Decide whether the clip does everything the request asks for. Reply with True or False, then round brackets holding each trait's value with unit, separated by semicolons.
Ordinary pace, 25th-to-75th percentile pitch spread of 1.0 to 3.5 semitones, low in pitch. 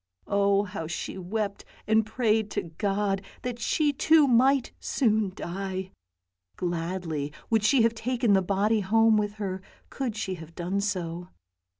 False (150 wpm; 3.2 semitones; 205 Hz)